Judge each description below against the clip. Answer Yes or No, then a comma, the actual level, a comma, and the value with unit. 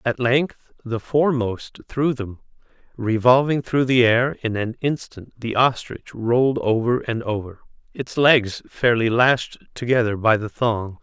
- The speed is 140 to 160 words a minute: Yes, average, 145 wpm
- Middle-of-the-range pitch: No, low, 120 Hz